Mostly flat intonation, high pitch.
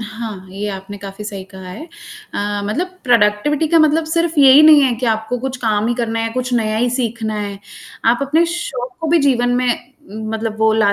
No: average, 4.7 semitones; high, 235 Hz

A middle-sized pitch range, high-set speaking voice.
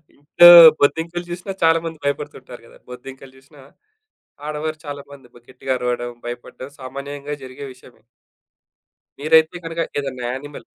No: average, 3.4 semitones; medium, 140 Hz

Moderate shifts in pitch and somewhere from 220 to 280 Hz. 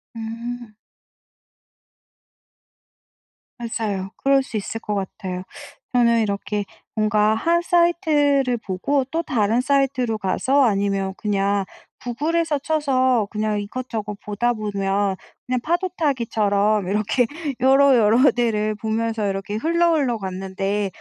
Yes: average, 4.7 semitones; high, 225 Hz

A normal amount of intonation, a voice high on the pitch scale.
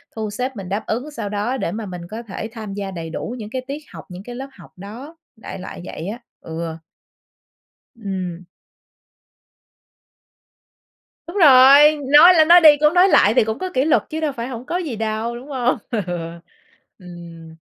No: wide, 5.9 semitones; high, 230 Hz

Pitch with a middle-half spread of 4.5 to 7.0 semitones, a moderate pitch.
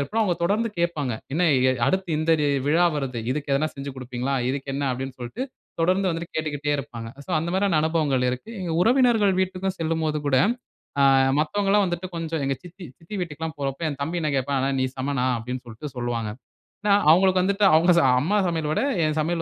Yes: average, 4.8 semitones; medium, 155 Hz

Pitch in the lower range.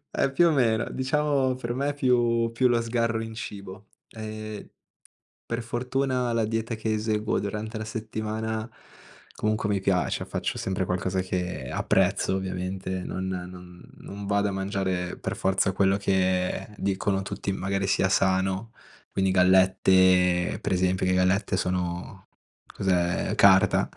Yes: low, 100 Hz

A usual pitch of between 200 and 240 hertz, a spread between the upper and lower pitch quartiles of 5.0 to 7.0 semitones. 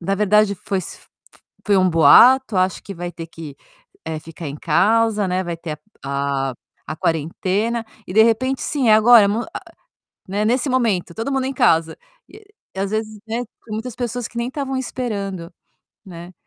Yes: high, 205 Hz; wide, 5.5 semitones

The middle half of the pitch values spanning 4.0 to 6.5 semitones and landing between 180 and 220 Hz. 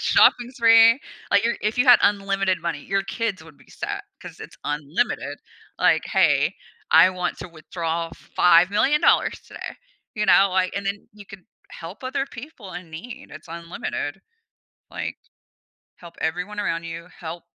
Yes: average, 4.5 semitones; high, 190 Hz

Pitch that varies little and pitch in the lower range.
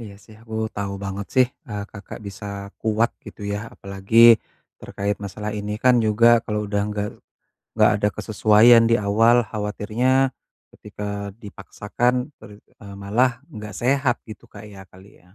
Yes: narrow, 2.3 semitones; low, 105 Hz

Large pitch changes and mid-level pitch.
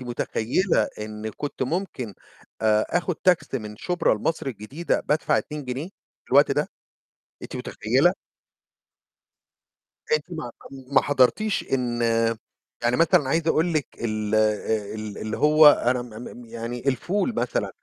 No: wide, 6.6 semitones; low, 125 Hz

